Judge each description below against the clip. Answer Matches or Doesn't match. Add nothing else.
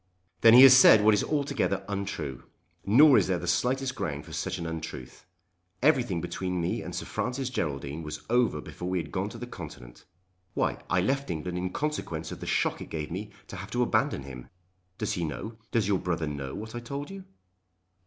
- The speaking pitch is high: Doesn't match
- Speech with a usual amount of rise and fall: Doesn't match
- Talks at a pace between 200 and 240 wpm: Matches